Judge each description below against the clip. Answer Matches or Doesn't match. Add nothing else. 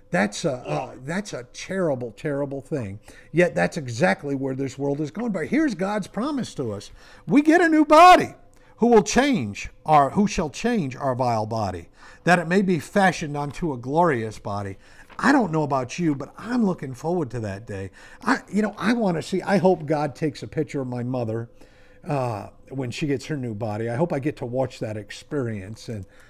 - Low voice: Doesn't match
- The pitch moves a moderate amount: Doesn't match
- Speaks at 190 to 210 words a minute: Matches